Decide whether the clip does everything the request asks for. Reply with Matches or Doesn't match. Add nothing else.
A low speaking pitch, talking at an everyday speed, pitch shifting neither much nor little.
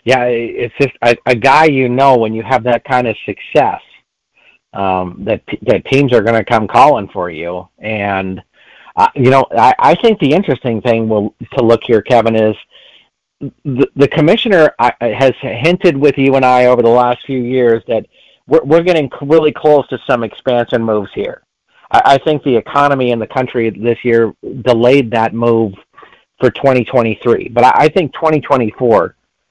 Matches